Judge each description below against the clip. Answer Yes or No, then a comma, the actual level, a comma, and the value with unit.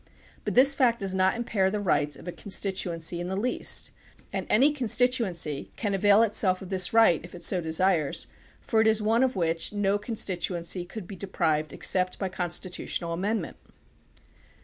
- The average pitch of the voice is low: No, high, 190 Hz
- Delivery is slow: No, average, 175 wpm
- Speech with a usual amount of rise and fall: Yes, average, 4.0 semitones